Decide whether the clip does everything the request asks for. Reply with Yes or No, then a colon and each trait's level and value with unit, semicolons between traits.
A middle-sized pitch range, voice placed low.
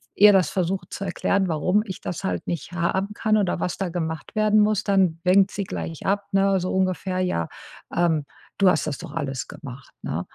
No: average, 3.2 semitones; medium, 185 Hz